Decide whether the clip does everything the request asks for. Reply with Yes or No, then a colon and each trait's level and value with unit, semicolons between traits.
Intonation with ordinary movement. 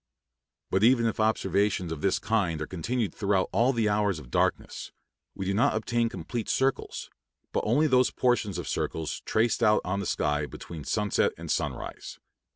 Yes: average, 4.0 semitones